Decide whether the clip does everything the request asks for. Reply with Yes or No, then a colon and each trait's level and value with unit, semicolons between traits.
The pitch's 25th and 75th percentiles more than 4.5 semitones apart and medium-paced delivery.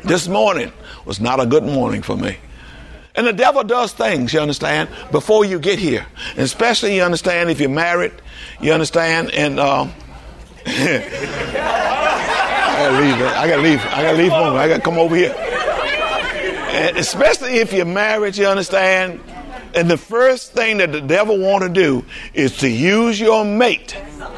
Yes: average, 5.1 semitones; average, 160 wpm